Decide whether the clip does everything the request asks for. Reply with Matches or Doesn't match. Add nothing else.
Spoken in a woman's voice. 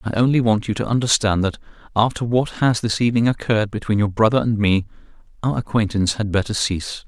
Doesn't match